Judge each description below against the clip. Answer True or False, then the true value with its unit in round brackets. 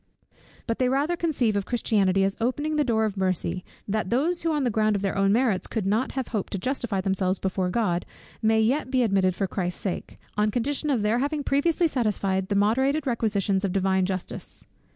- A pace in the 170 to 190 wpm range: False (205 wpm)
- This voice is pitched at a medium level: False (215 Hz)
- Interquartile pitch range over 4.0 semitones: True (5.1 semitones)